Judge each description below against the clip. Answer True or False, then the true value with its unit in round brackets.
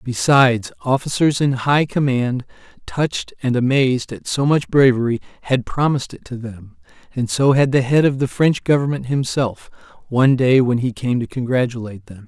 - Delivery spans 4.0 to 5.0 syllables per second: False (5.2 syllables/s)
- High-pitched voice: False (130 Hz)